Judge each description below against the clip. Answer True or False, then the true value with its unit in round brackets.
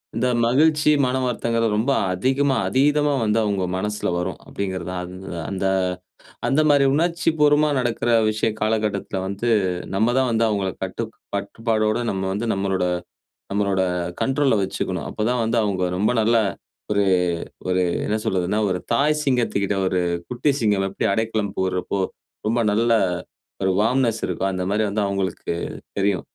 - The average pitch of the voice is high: False (110 Hz)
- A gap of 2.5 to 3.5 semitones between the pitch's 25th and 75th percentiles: False (4.2 semitones)